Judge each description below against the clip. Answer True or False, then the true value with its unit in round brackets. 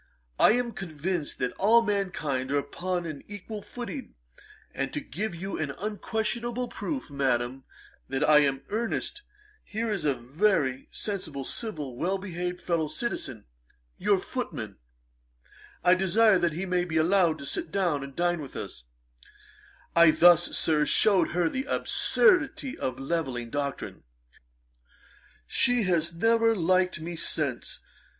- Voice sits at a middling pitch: True (175 Hz)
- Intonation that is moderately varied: False (6.1 semitones)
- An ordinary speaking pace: True (145 wpm)